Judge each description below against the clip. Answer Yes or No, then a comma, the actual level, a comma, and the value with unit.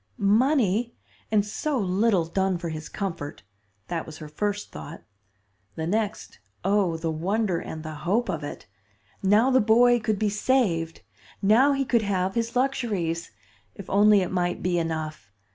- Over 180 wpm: No, average, 160 wpm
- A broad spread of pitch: No, average, 5.0 semitones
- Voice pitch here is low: No, high, 195 Hz